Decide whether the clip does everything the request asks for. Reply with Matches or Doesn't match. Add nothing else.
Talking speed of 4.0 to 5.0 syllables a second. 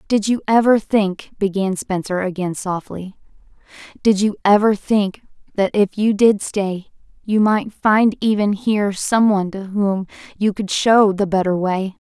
Matches